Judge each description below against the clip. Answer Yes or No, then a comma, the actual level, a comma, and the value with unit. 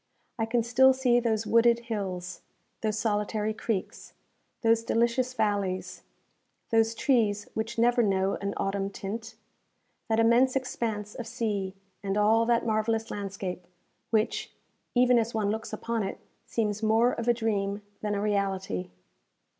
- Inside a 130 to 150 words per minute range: Yes, average, 140 wpm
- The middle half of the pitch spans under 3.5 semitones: Yes, narrow, 2.5 semitones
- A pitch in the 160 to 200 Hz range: No, high, 220 Hz